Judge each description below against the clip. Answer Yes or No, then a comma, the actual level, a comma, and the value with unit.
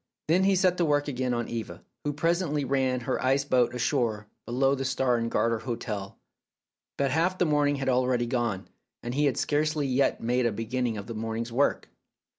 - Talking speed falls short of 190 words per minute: No, average, 195 wpm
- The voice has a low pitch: Yes, low, 130 Hz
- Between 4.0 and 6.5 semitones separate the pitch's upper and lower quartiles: No, average, 3.5 semitones